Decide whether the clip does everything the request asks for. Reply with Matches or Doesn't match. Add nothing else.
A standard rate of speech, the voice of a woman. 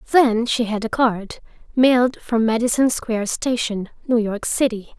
Matches